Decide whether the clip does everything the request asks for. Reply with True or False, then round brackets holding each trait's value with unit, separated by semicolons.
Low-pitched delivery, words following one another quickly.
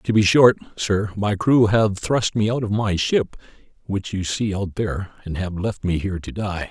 True (100 Hz; 225 wpm)